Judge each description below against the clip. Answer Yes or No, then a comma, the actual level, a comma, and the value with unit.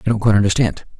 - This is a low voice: Yes, low, 105 Hz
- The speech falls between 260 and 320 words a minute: No, fast, 240 wpm